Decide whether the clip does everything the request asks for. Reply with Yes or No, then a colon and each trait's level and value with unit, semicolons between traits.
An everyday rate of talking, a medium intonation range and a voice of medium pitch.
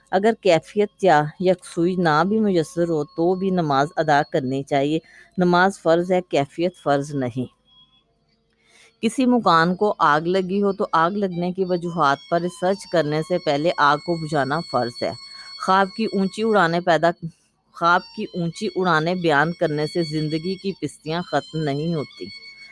Yes: average, 155 wpm; average, 3.7 semitones; medium, 170 Hz